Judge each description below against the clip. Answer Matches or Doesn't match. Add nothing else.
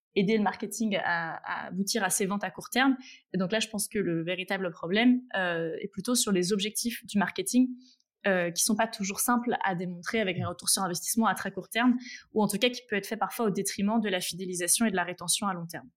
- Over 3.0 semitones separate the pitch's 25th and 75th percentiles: Matches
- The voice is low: Doesn't match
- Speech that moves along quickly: Matches